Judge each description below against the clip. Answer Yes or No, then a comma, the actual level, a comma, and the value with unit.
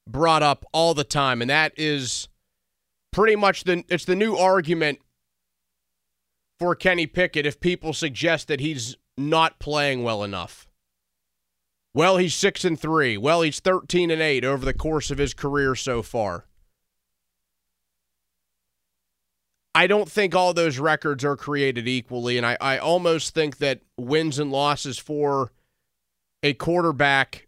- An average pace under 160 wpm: Yes, average, 145 wpm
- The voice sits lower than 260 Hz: Yes, medium, 140 Hz